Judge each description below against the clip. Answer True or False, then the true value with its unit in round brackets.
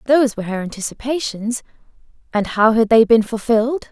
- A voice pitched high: True (230 Hz)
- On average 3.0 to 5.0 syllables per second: False (5.9 syllables/s)